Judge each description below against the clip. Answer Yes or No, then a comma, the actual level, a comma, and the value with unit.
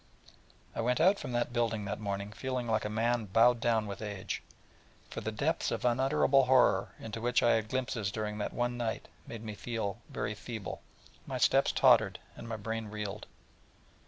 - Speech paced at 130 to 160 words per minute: No, average, 190 wpm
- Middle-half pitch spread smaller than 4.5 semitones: Yes, narrow, 2.5 semitones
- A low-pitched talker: Yes, low, 115 Hz